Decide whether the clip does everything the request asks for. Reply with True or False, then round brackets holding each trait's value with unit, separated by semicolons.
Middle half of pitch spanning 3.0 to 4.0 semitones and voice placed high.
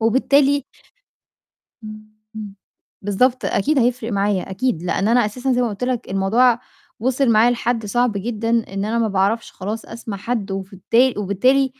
True (3.7 semitones; 225 Hz)